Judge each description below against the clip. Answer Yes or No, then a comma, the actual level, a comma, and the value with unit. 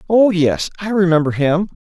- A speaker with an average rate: Yes, average, 165 wpm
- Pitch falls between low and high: Yes, medium, 180 Hz